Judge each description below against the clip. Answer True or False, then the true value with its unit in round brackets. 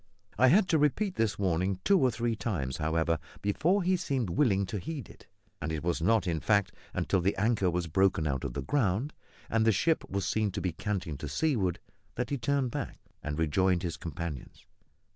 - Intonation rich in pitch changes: True (7.1 semitones)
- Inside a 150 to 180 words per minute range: False (200 wpm)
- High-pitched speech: False (100 Hz)